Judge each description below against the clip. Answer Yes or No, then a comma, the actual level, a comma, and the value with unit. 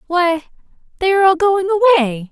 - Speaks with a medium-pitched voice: No, very high, 350 Hz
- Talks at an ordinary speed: Yes, average, 155 wpm